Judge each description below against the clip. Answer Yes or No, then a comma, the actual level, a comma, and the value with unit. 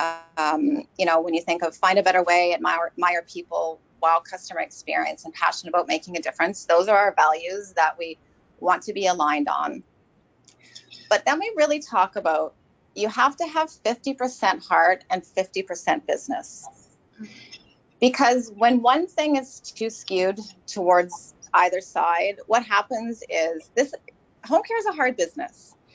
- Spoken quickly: No, average, 160 wpm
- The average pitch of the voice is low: No, medium, 185 Hz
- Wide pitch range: Yes, wide, 6.4 semitones